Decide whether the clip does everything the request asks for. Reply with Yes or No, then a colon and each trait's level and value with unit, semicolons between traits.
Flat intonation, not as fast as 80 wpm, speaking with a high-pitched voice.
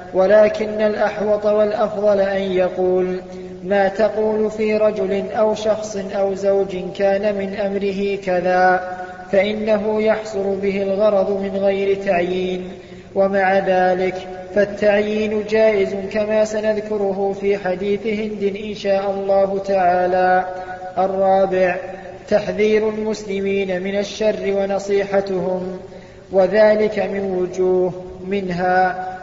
No: narrow, 2.1 semitones; average, 95 wpm; high, 195 Hz